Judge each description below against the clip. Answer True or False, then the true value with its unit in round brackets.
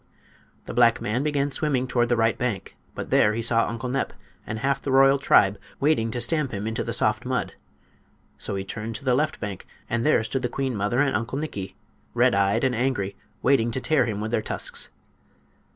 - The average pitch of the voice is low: True (120 Hz)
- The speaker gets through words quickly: True (210 wpm)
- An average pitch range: True (3.6 semitones)